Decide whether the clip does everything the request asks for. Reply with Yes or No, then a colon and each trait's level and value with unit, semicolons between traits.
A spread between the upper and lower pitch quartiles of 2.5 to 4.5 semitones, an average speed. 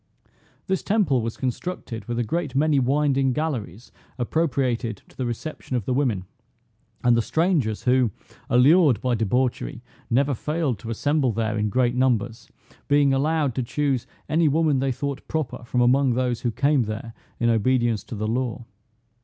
Yes: average, 3.5 semitones; average, 160 wpm